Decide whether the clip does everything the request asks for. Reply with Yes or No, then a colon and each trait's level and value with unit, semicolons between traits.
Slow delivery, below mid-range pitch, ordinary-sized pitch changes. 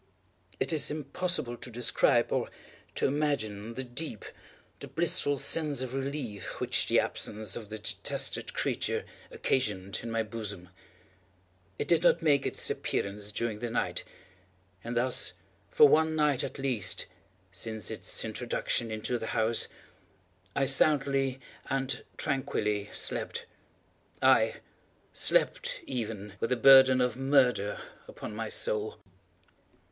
Yes: slow, 130 wpm; low, 125 Hz; average, 4.1 semitones